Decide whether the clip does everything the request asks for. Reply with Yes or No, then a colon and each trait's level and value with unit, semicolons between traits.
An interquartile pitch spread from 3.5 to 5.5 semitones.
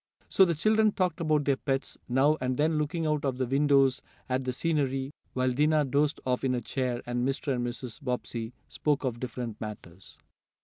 No: average, 3.1 semitones